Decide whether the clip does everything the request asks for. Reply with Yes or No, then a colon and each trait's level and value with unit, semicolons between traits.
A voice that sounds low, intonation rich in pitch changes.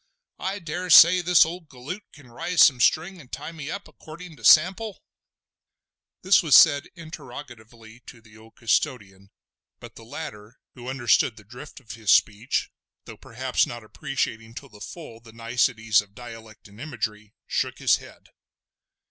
Yes: low, 125 Hz; wide, 6.0 semitones